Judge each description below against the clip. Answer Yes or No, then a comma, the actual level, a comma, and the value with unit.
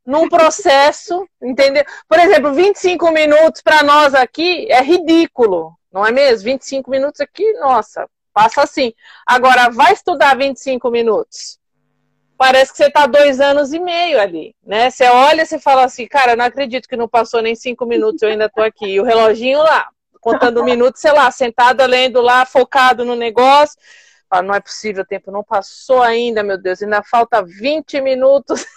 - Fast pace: No, average, 175 wpm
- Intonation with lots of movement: No, average, 4.1 semitones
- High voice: Yes, very high, 260 Hz